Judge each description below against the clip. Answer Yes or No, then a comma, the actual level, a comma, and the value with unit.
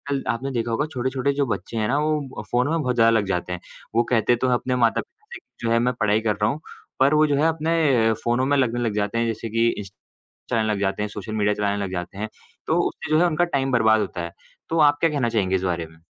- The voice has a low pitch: Yes, low, 115 Hz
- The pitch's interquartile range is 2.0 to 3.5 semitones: No, average, 4.8 semitones